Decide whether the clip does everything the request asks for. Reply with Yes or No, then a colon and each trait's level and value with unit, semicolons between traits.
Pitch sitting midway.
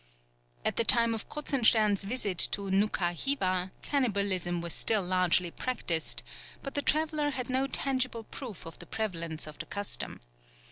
No: high, 210 Hz